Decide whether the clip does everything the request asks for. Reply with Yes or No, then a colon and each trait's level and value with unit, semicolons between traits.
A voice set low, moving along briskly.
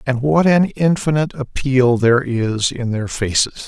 No: low, 130 Hz; average, 165 wpm